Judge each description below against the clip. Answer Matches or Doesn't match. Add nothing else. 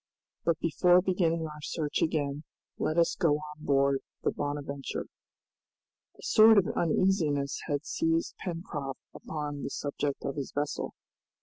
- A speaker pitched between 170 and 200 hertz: Doesn't match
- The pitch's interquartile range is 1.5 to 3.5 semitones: Matches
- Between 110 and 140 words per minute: Matches